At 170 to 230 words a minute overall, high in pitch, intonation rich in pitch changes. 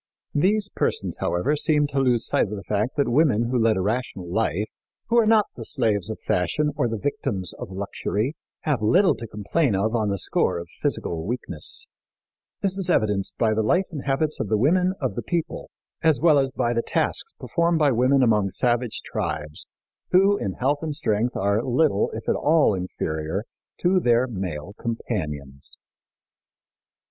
No: average, 180 wpm; low, 120 Hz; wide, 6.9 semitones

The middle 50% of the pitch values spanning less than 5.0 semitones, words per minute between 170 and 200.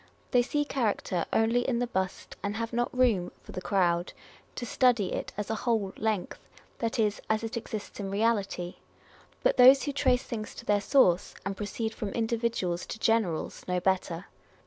Yes: average, 3.7 semitones; average, 180 wpm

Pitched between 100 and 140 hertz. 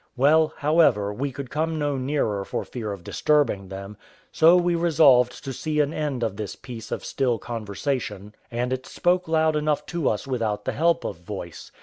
Yes: low, 135 Hz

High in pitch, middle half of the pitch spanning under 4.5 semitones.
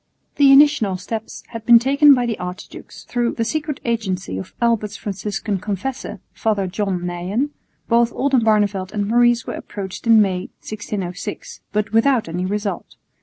Yes: high, 215 Hz; average, 3.6 semitones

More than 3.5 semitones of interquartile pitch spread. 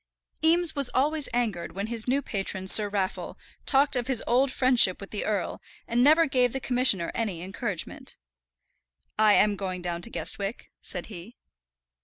Yes: average, 5.1 semitones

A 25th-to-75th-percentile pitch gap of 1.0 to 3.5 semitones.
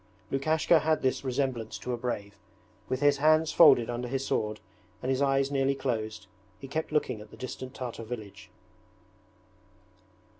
Yes: average, 3.2 semitones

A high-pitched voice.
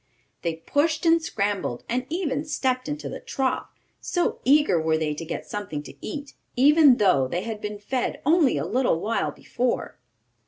Yes: very high, 250 Hz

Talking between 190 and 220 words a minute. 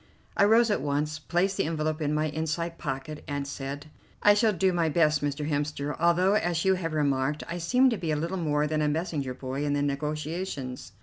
Yes: fast, 205 wpm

